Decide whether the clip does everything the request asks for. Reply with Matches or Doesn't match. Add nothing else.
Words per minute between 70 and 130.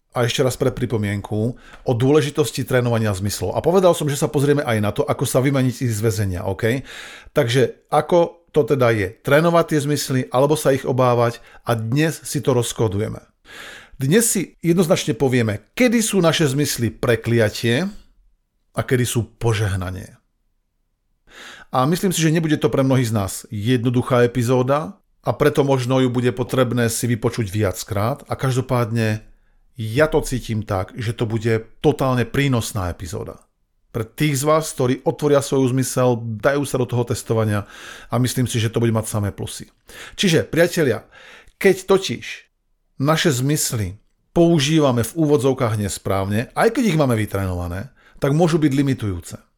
Doesn't match